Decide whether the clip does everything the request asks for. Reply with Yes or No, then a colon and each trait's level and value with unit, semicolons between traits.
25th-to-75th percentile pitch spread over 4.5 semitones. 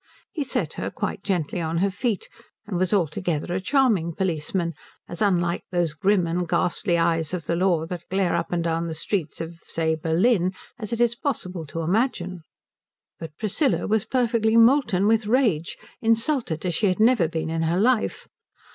Yes: average, 4.9 semitones